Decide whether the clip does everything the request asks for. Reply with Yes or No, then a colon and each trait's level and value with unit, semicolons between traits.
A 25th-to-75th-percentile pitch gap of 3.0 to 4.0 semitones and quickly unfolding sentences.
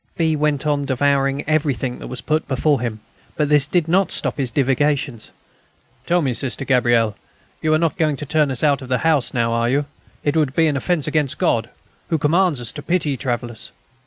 Yes: average, 3.3 semitones; fast, 220 wpm